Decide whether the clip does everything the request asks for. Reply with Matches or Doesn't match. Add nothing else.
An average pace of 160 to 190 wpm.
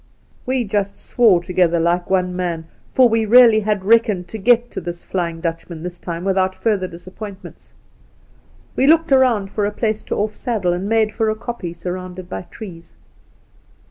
Matches